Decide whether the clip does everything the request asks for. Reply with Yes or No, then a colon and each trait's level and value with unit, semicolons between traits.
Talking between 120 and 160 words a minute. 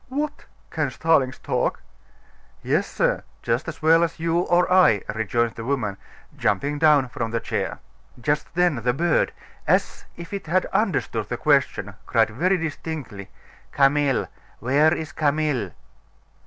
Yes: average, 140 wpm